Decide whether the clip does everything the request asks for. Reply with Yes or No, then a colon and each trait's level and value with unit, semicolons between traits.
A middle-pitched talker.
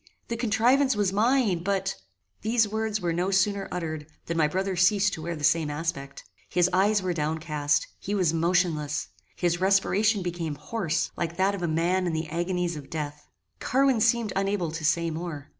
Yes: medium, 180 Hz